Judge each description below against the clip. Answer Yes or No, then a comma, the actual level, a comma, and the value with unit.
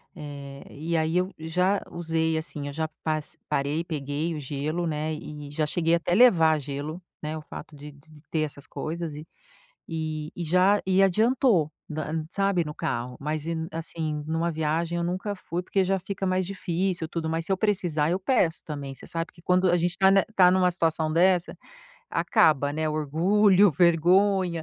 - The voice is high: No, medium, 165 Hz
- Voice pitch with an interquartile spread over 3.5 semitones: No, average, 3.0 semitones